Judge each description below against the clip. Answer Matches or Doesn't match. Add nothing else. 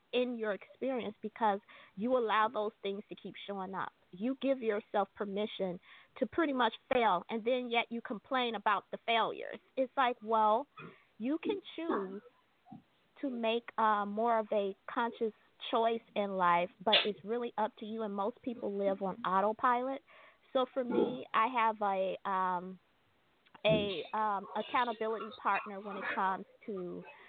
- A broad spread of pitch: Doesn't match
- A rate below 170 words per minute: Matches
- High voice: Matches